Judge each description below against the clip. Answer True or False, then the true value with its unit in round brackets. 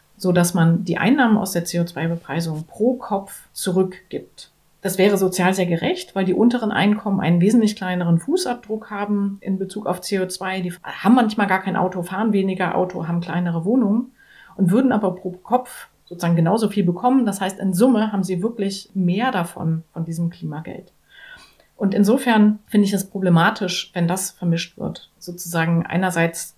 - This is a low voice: False (190 Hz)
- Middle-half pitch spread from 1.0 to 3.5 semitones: True (3.2 semitones)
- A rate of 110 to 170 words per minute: True (165 wpm)